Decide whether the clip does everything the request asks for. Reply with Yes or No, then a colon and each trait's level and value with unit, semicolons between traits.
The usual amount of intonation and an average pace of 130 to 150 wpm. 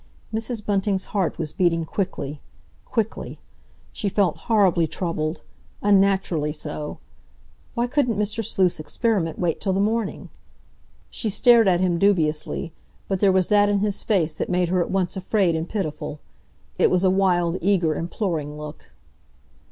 Yes: average, 3.6 semitones; average, 145 wpm